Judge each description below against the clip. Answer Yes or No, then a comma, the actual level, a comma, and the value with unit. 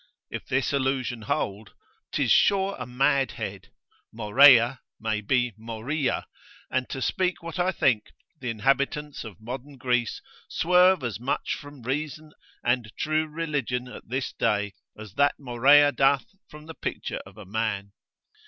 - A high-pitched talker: No, low, 130 Hz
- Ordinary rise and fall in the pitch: Yes, average, 4.3 semitones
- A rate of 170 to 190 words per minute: No, average, 145 wpm